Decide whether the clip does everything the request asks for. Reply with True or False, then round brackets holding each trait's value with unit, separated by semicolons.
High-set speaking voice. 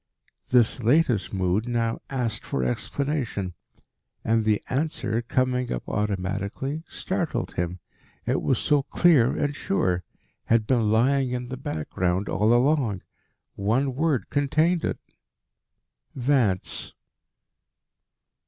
False (120 Hz)